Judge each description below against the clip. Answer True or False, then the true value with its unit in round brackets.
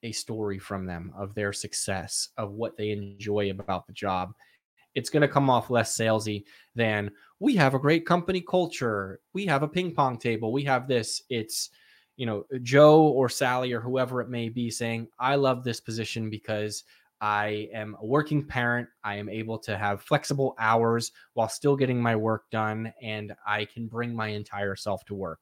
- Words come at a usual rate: True (190 wpm)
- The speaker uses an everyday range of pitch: True (3.5 semitones)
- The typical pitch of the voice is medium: False (115 Hz)